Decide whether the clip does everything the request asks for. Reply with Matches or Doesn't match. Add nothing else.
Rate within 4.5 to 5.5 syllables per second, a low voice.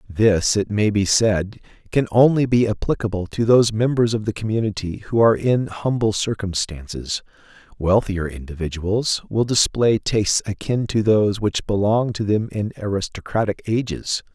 Matches